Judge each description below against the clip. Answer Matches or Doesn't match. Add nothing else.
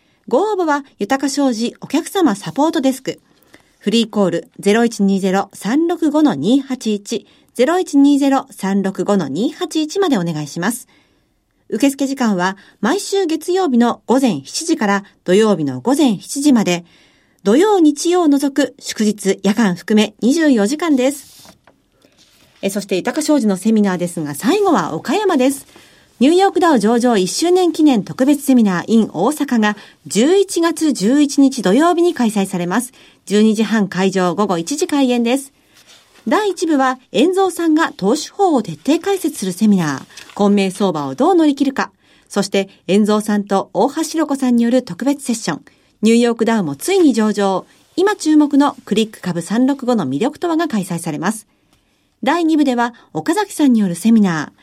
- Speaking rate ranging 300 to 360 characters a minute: Doesn't match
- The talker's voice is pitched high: Matches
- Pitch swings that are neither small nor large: Doesn't match